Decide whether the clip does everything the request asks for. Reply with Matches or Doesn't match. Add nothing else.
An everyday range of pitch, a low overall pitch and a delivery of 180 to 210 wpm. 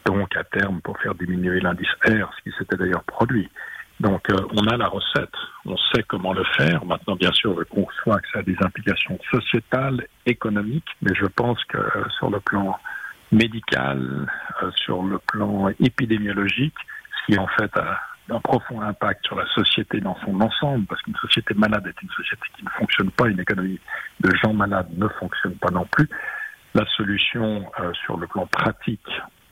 Matches